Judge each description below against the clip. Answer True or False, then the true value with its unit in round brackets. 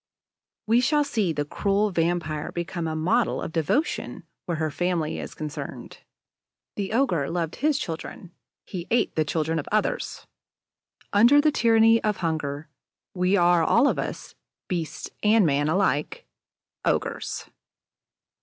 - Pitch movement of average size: False (5.7 semitones)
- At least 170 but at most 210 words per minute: False (135 wpm)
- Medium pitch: True (175 Hz)